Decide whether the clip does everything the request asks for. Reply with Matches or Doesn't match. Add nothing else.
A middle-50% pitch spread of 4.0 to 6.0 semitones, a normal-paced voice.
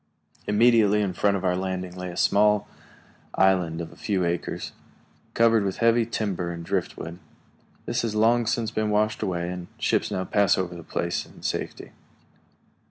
Doesn't match